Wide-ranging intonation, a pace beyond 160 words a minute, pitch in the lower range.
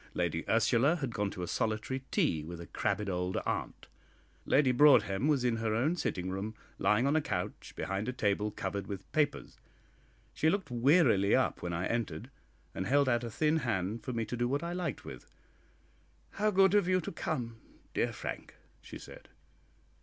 Yes: wide, 6.6 semitones; average, 185 wpm; low, 115 Hz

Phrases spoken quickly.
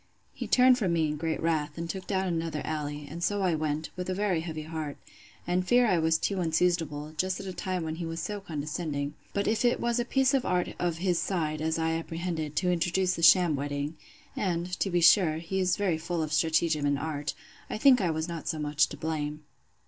Yes: fast, 230 wpm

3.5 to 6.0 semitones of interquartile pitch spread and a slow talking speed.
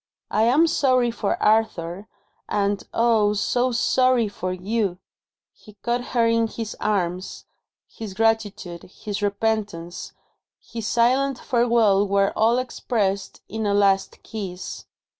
No: average, 2.9 semitones; slow, 120 wpm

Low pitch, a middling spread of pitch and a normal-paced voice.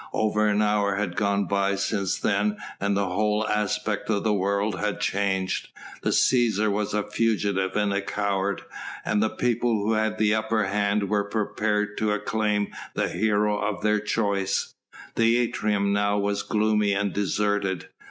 No: low, 105 Hz; narrow, 1.1 semitones; average, 160 wpm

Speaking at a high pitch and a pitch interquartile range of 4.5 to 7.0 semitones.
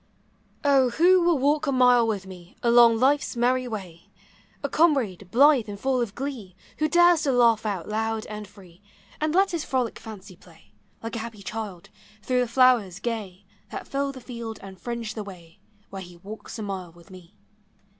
Yes: high, 225 Hz; average, 4.9 semitones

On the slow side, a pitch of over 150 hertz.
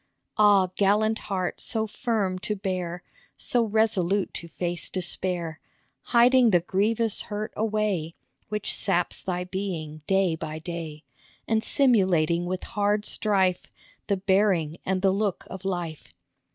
Yes: slow, 130 wpm; high, 190 Hz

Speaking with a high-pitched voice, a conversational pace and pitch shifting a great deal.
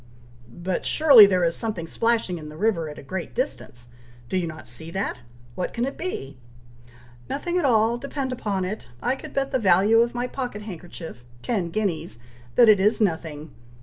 Yes: high, 200 Hz; average, 185 wpm; wide, 6.3 semitones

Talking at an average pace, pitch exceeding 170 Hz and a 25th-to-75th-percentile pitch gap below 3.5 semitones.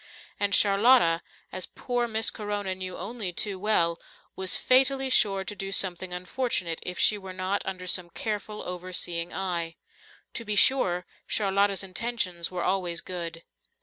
Yes: average, 150 wpm; high, 190 Hz; average, 2.8 semitones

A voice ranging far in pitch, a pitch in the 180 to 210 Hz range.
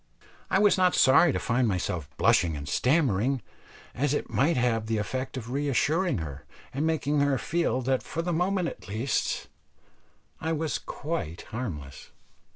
No: wide, 6.5 semitones; low, 130 Hz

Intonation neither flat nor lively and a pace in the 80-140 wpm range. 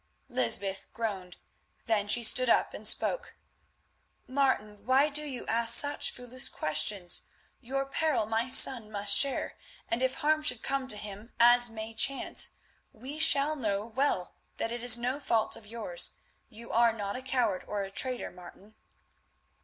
No: average, 4.0 semitones; average, 160 wpm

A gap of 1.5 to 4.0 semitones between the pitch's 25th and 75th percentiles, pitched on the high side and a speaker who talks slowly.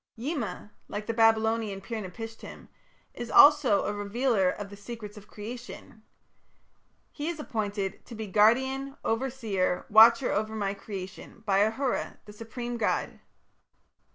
Yes: average, 2.8 semitones; high, 220 Hz; slow, 130 wpm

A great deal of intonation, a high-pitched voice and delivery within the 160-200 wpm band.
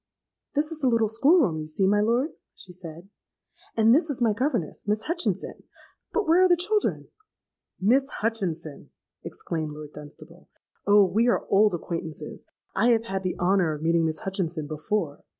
Yes: wide, 6.8 semitones; high, 205 Hz; average, 170 wpm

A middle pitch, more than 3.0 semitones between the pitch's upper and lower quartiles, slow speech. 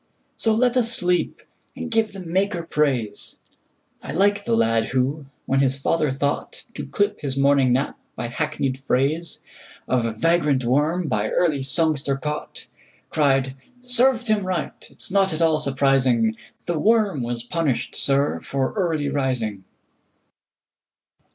Yes: medium, 145 Hz; wide, 5.4 semitones; slow, 125 wpm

